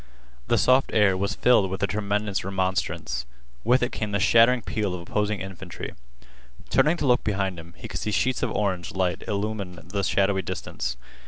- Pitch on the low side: Yes, low, 100 Hz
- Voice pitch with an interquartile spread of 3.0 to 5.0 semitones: No, narrow, 2.5 semitones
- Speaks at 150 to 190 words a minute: Yes, average, 180 wpm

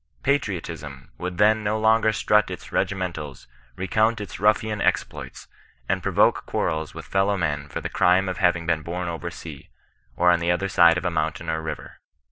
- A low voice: Yes, very low, 90 Hz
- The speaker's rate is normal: Yes, average, 190 wpm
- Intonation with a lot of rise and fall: No, average, 3.9 semitones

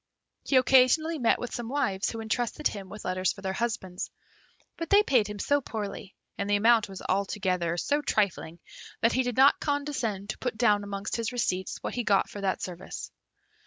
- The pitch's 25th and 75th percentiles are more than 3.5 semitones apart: Yes, average, 4.3 semitones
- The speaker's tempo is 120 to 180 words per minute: No, average, 195 wpm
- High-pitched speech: Yes, high, 215 Hz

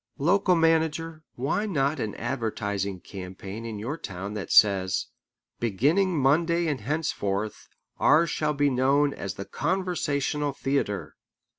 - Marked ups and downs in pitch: Yes, wide, 7.5 semitones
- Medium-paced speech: No, slow, 125 wpm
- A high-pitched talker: No, medium, 140 Hz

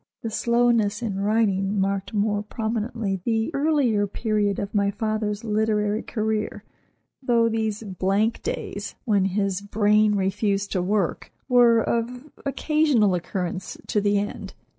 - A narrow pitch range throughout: Yes, narrow, 2.2 semitones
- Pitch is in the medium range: No, high, 210 Hz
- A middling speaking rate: No, slow, 130 wpm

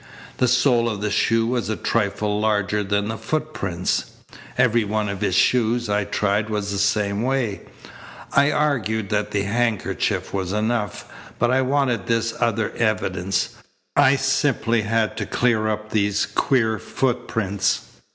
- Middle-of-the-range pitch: No, low, 110 Hz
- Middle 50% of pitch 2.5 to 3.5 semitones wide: Yes, average, 2.8 semitones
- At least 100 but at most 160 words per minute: Yes, average, 150 wpm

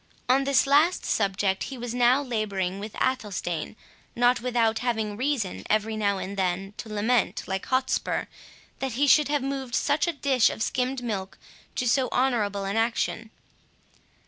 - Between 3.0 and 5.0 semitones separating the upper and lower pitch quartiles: Yes, average, 4.2 semitones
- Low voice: No, high, 235 Hz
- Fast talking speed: No, average, 160 wpm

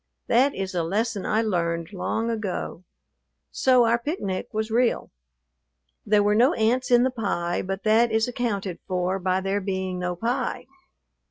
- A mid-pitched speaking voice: No, high, 210 Hz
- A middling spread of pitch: Yes, average, 3.9 semitones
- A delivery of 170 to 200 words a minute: No, average, 160 wpm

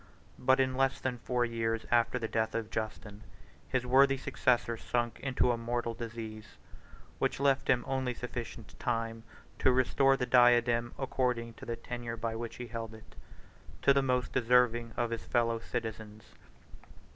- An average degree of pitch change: No, narrow, 1.7 semitones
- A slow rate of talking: No, average, 160 wpm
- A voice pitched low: Yes, low, 120 Hz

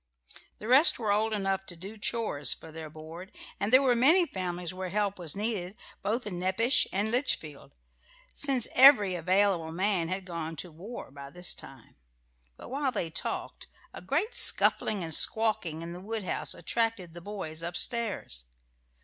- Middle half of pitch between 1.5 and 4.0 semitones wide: No, average, 5.0 semitones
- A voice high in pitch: Yes, high, 195 Hz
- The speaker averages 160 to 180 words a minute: Yes, average, 165 wpm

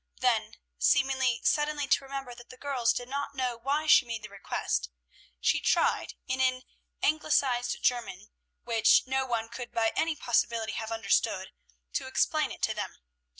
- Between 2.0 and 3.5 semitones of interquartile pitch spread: Yes, average, 3.0 semitones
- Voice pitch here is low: No, high, 245 Hz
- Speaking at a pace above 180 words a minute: No, average, 160 wpm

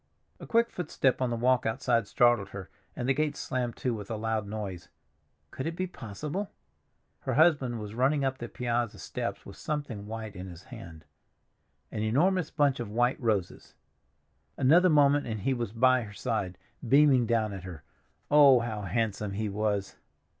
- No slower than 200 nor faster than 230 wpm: No, average, 170 wpm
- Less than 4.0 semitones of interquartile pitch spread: No, average, 4.5 semitones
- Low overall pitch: Yes, low, 120 Hz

